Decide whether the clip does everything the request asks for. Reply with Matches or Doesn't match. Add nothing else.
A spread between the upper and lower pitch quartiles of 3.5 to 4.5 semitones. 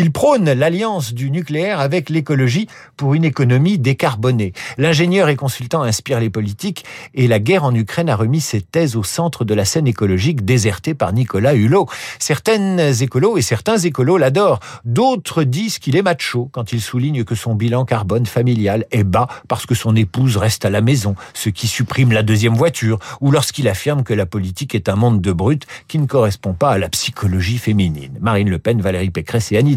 Doesn't match